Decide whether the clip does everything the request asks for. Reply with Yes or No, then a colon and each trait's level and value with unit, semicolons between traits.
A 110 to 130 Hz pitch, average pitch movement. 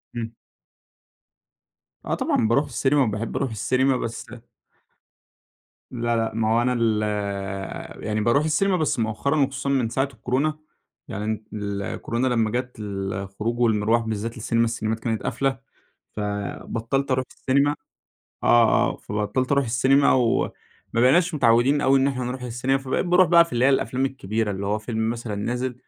Yes: low, 120 Hz; average, 3.3 semitones